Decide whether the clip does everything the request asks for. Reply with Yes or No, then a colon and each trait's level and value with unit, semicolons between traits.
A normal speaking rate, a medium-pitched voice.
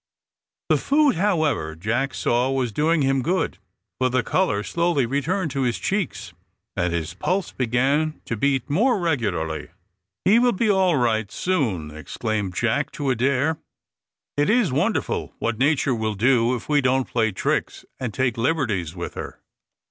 No: average, 155 wpm; low, 130 Hz